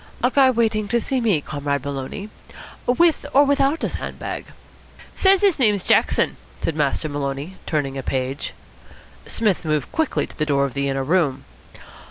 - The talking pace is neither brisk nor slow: Yes, average, 170 wpm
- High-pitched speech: No, medium, 165 Hz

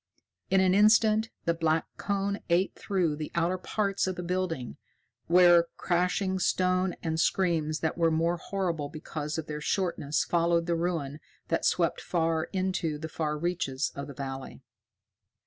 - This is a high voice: No, medium, 170 Hz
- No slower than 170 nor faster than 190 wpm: No, average, 155 wpm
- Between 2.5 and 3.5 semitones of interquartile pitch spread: Yes, average, 2.9 semitones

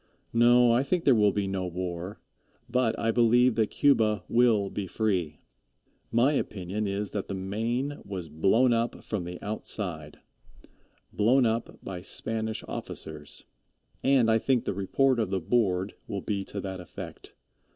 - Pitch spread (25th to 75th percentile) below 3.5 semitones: No, average, 4.0 semitones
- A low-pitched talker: Yes, low, 105 Hz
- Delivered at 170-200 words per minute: No, average, 155 wpm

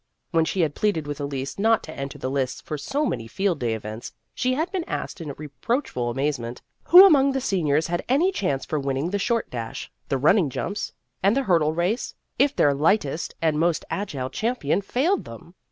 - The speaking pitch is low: No, medium, 165 Hz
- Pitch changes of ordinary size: No, wide, 8.4 semitones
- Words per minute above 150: Yes, average, 200 wpm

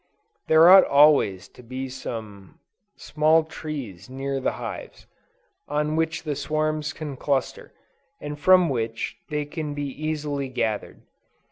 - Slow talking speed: Yes, slow, 130 wpm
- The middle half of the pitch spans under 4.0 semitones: Yes, average, 3.0 semitones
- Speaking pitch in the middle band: Yes, medium, 145 Hz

